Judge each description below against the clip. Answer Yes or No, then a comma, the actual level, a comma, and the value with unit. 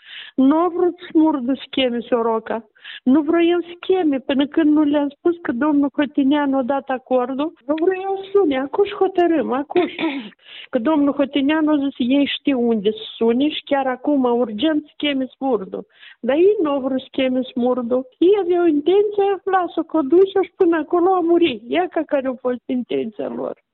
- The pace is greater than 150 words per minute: Yes, fast, 170 wpm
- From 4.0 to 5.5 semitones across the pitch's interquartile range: Yes, average, 4.6 semitones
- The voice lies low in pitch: No, very high, 295 Hz